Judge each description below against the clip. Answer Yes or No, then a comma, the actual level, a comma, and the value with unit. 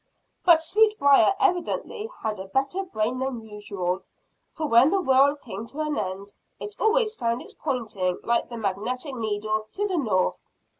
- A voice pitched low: No, very high, 255 Hz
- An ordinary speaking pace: Yes, average, 160 wpm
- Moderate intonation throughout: No, wide, 7.5 semitones